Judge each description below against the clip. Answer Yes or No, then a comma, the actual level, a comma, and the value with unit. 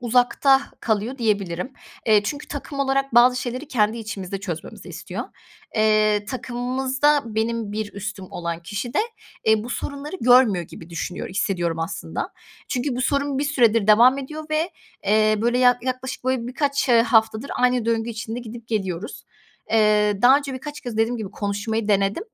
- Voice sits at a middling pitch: No, high, 230 Hz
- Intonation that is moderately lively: Yes, average, 3.7 semitones